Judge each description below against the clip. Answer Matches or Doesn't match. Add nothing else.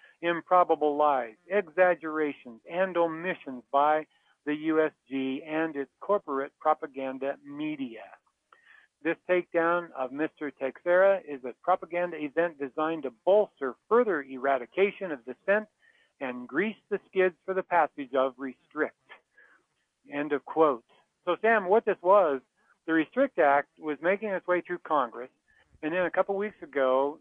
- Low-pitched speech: Doesn't match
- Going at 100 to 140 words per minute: Matches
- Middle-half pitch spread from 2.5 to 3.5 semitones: Doesn't match